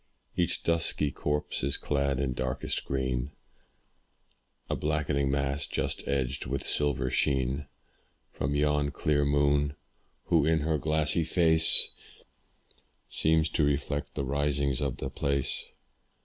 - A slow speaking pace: Yes, slow, 120 wpm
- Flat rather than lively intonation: Yes, narrow, 1.7 semitones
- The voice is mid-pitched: No, very low, 70 Hz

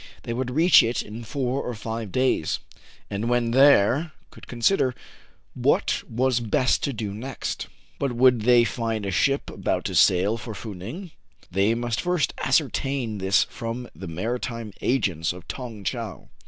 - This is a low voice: Yes, low, 115 Hz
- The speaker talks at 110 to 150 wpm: No, average, 160 wpm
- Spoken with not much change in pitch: No, average, 3.6 semitones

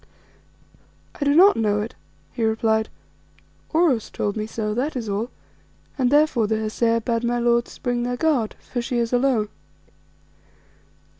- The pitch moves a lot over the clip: No, narrow, 2.4 semitones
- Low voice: No, high, 235 Hz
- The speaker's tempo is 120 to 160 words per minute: Yes, average, 150 wpm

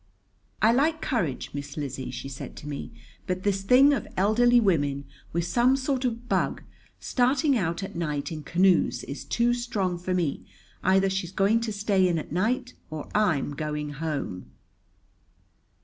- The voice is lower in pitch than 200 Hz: Yes, high, 190 Hz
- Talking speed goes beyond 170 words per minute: No, average, 165 wpm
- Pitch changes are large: Yes, wide, 7.6 semitones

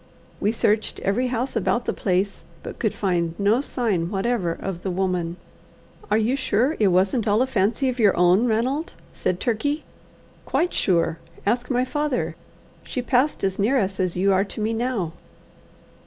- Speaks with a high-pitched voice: Yes, high, 215 Hz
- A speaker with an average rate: Yes, average, 170 wpm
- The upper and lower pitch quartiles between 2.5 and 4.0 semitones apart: No, average, 4.8 semitones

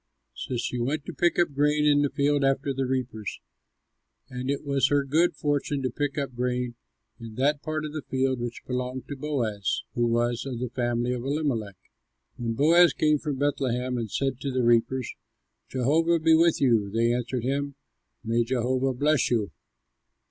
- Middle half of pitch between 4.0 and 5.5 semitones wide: No, average, 3.1 semitones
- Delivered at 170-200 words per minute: Yes, average, 180 wpm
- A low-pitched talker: Yes, low, 130 Hz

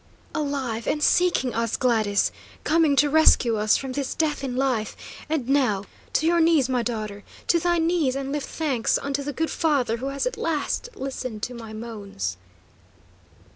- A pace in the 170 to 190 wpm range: Yes, average, 175 wpm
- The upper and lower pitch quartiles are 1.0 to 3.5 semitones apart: No, average, 4.7 semitones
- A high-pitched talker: Yes, very high, 270 Hz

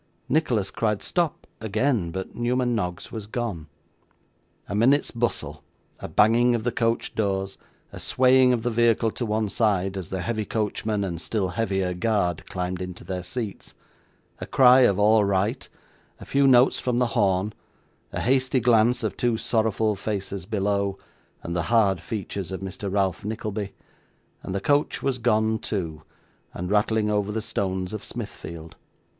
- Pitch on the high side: No, low, 105 Hz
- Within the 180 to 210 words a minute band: No, average, 160 wpm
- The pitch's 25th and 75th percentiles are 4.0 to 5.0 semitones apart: No, average, 3.6 semitones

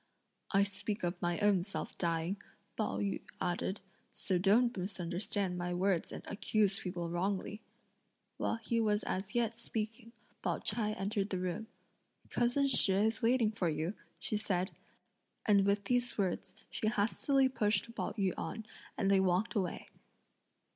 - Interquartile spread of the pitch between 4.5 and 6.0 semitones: No, average, 3.1 semitones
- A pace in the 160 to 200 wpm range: No, average, 150 wpm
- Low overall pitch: No, high, 200 Hz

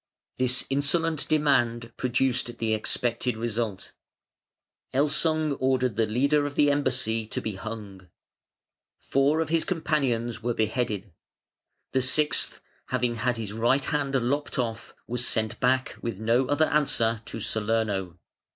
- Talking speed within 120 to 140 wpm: Yes, slow, 135 wpm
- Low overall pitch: Yes, low, 125 Hz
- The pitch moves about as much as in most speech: Yes, average, 3.9 semitones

